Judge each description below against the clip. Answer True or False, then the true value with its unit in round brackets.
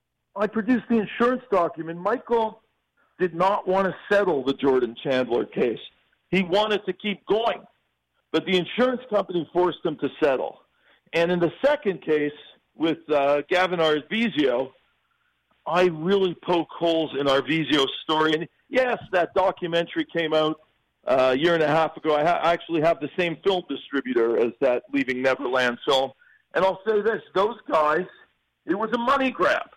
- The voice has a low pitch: False (170 Hz)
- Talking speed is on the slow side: False (165 wpm)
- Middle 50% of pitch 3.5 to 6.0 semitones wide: True (5.0 semitones)